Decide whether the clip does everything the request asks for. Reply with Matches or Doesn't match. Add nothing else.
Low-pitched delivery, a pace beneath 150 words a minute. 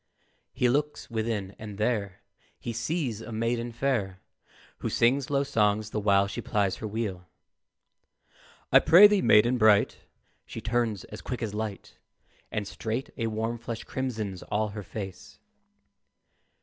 Matches